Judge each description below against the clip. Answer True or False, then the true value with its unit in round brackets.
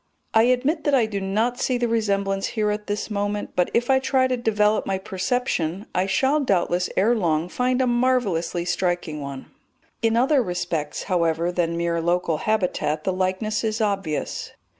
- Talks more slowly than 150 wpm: False (175 wpm)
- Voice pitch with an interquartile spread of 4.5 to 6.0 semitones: True (5.2 semitones)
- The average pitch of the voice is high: True (205 Hz)